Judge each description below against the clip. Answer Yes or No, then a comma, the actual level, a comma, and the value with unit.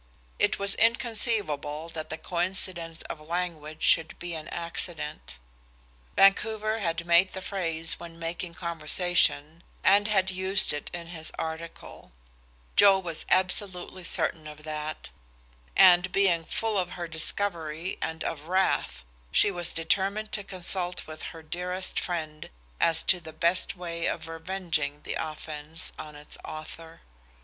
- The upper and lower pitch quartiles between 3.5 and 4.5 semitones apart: No, average, 2.8 semitones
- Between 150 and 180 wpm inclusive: No, average, 140 wpm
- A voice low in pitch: No, medium, 170 Hz